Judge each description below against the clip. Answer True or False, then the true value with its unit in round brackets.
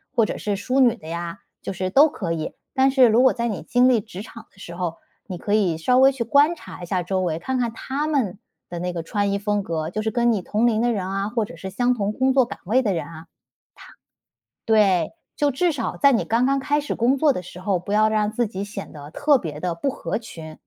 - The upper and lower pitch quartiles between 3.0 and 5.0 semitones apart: False (5.6 semitones)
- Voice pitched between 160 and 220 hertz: True (215 Hz)